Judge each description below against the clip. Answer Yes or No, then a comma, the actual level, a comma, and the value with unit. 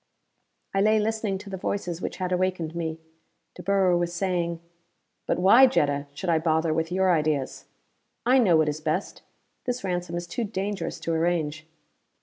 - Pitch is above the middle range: No, medium, 175 Hz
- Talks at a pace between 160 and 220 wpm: Yes, average, 170 wpm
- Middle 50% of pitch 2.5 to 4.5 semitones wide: Yes, average, 3.3 semitones